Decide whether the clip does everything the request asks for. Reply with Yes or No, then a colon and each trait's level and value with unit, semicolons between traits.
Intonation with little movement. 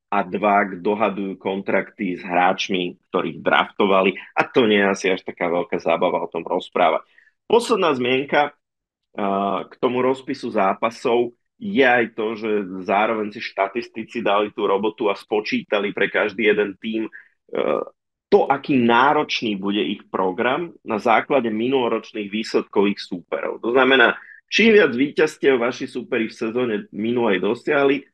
No: average, 3.7 semitones